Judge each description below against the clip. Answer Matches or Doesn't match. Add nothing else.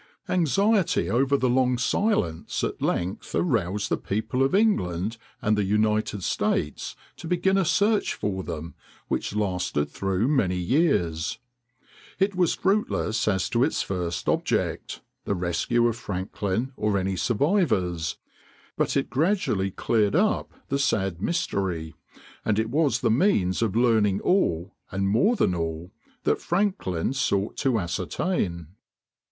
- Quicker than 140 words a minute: Doesn't match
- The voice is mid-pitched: Doesn't match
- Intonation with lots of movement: Matches